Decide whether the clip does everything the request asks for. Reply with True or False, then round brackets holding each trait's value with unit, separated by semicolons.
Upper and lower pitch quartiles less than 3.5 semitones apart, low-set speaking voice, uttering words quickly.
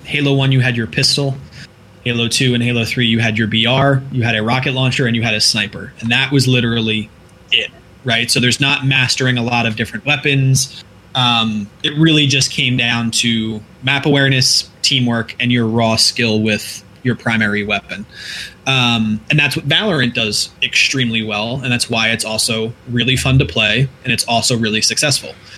False (3.1 semitones; 120 Hz; 190 wpm)